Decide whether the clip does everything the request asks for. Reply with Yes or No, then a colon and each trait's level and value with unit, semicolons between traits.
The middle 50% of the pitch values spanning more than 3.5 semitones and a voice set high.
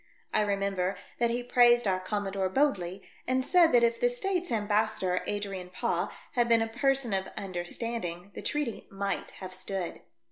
Yes: average, 4.2 semitones; high, 210 Hz